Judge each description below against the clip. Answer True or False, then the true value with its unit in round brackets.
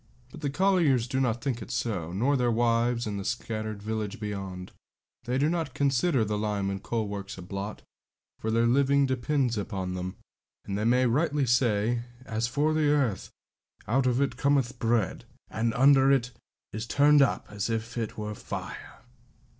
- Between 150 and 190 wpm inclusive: True (175 wpm)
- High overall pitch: False (120 Hz)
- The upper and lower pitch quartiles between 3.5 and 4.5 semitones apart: True (4.2 semitones)